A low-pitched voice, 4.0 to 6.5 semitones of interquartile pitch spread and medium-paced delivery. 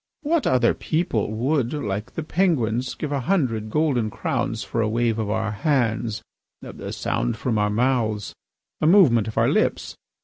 Yes: low, 120 Hz; wide, 5.5 semitones; average, 165 wpm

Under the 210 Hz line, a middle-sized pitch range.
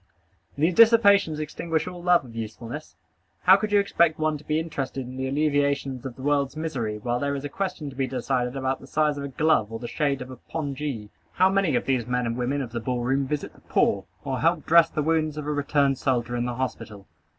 Yes: medium, 140 Hz; average, 3.7 semitones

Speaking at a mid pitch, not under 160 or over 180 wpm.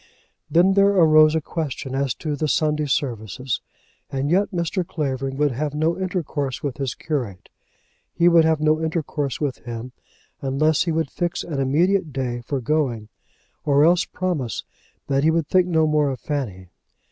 Yes: medium, 150 Hz; average, 170 wpm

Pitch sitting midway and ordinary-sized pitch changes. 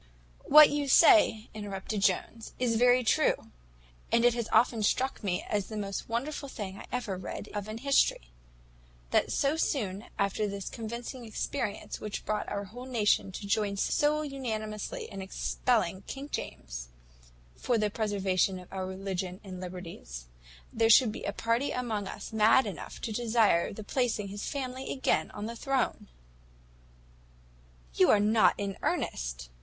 No: high, 215 Hz; average, 3.9 semitones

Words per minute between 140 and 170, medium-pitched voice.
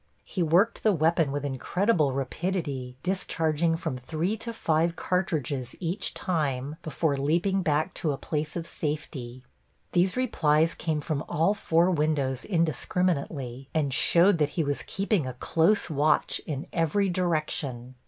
Yes: average, 145 wpm; medium, 160 Hz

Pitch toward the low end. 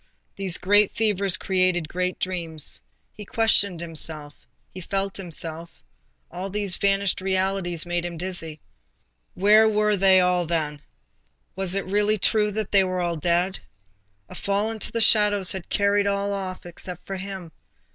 No: high, 190 Hz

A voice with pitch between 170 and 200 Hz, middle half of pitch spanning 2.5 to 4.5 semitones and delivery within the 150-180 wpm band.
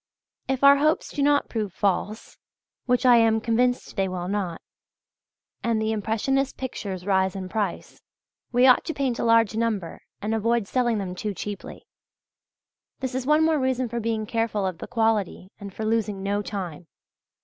No: high, 220 Hz; average, 3.8 semitones; average, 170 wpm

